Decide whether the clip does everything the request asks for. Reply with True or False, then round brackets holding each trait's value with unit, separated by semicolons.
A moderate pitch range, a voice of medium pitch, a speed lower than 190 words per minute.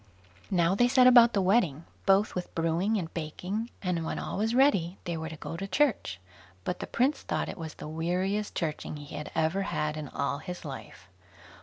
False (4.6 semitones; 180 Hz; 195 wpm)